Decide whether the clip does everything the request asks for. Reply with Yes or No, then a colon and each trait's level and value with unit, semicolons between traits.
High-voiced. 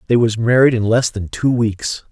No: low, 115 Hz